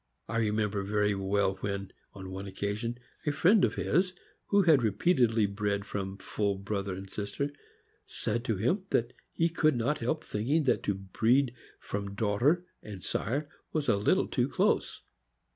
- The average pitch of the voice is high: No, low, 105 Hz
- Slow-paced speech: No, average, 160 wpm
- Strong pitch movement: Yes, wide, 5.9 semitones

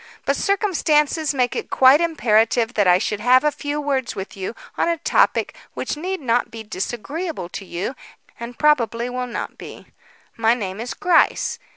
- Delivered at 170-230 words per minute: Yes, average, 175 wpm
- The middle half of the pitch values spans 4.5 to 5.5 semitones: Yes, average, 5.1 semitones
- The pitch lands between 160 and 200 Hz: No, very high, 250 Hz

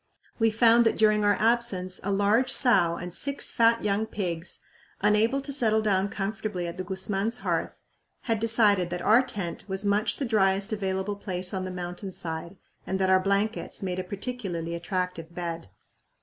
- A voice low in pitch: No, high, 200 Hz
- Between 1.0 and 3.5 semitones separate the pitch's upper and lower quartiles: Yes, average, 3.2 semitones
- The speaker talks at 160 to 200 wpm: Yes, average, 175 wpm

